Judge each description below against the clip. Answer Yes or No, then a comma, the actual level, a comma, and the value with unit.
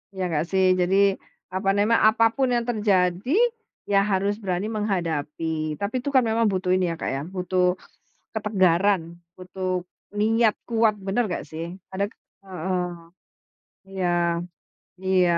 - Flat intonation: No, average, 3.0 semitones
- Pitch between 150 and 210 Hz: Yes, high, 190 Hz